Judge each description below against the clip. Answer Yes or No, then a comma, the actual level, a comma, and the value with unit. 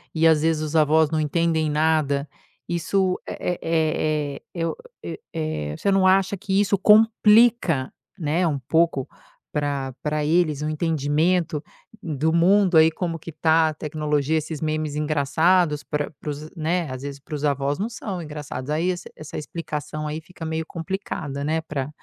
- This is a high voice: No, medium, 155 Hz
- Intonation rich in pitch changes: No, narrow, 2.4 semitones